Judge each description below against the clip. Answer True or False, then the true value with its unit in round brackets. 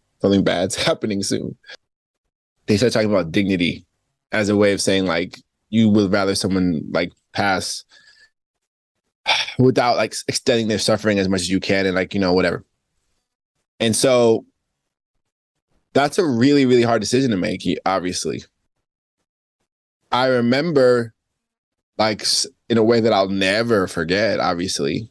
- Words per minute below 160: True (140 wpm)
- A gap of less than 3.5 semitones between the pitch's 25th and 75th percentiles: False (3.9 semitones)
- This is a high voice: False (105 Hz)